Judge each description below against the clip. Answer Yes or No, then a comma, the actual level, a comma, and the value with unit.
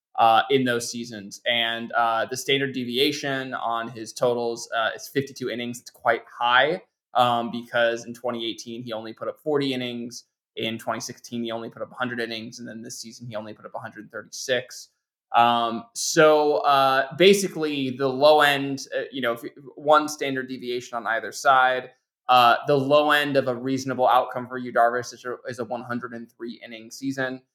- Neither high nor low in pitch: No, low, 125 Hz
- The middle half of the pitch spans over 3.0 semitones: No, narrow, 2.4 semitones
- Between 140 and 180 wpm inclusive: Yes, average, 175 wpm